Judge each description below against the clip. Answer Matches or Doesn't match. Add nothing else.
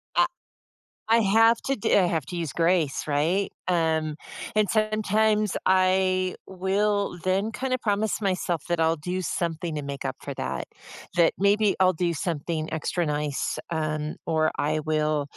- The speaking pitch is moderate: Matches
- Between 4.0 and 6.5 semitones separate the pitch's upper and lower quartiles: Matches